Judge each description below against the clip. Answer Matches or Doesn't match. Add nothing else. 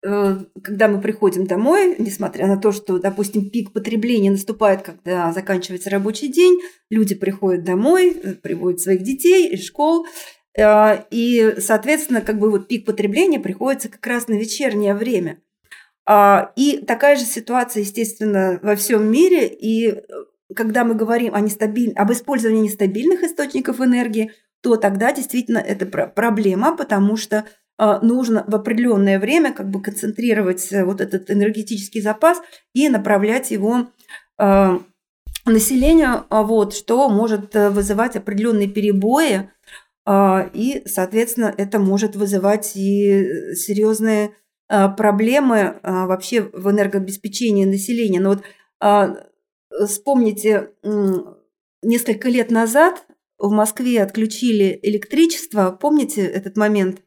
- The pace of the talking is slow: Doesn't match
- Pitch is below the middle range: Doesn't match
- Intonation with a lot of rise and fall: Doesn't match